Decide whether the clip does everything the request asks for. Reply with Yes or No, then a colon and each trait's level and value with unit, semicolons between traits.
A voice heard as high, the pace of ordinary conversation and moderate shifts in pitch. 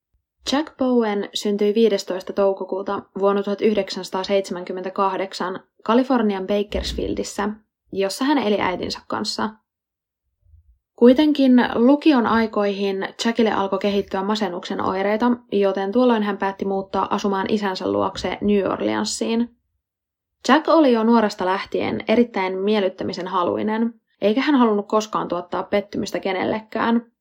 Yes: high, 200 Hz; average, 105 wpm; average, 3.2 semitones